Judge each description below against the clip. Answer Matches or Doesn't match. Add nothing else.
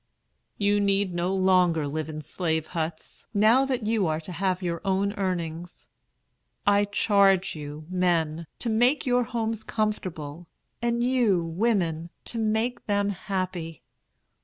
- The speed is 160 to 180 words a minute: Doesn't match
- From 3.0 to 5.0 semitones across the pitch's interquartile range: Matches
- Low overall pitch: Doesn't match